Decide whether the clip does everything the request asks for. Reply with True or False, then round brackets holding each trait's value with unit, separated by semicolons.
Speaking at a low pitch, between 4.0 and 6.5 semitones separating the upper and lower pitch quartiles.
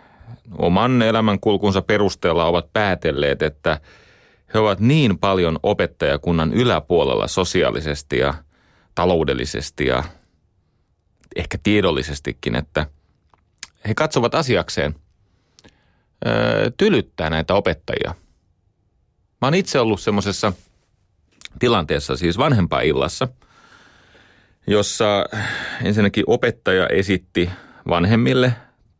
True (95 Hz; 4.3 semitones)